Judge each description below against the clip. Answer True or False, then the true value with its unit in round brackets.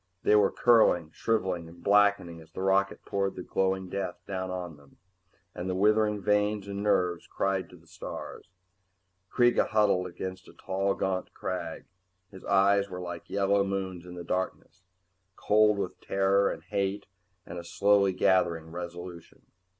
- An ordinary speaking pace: True (160 wpm)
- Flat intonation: True (2.1 semitones)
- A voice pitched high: False (95 Hz)